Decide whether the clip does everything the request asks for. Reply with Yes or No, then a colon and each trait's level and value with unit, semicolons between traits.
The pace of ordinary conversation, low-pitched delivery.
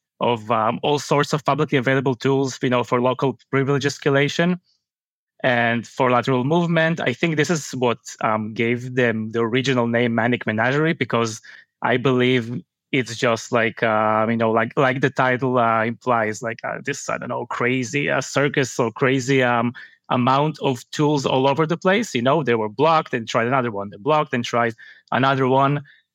Yes: average, 185 wpm; low, 130 Hz